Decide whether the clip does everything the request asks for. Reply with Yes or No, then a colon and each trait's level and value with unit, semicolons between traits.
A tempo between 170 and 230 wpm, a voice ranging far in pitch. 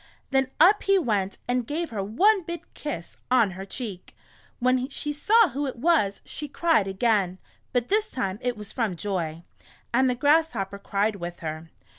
Yes: average, 175 wpm; wide, 7.2 semitones